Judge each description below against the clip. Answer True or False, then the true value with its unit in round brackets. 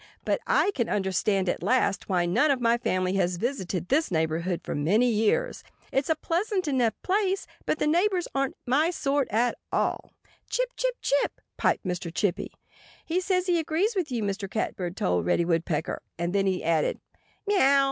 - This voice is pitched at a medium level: False (235 Hz)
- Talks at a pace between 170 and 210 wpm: True (180 wpm)